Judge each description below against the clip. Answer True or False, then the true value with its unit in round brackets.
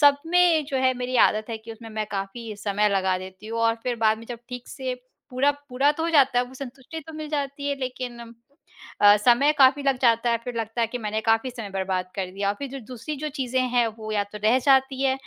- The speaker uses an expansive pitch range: False (3.7 semitones)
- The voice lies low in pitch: False (245 Hz)